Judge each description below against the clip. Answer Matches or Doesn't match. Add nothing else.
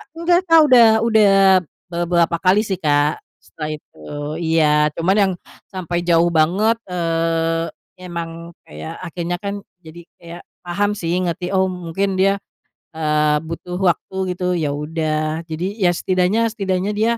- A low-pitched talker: Doesn't match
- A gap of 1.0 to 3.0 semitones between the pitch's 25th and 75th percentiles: Matches